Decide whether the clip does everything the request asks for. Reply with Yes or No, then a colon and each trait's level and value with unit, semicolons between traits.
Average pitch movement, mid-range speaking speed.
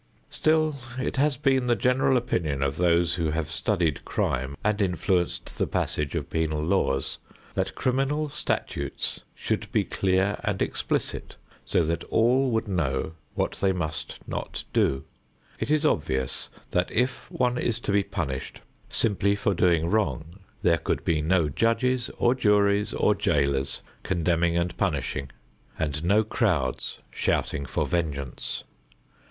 No: wide, 6.5 semitones; average, 145 wpm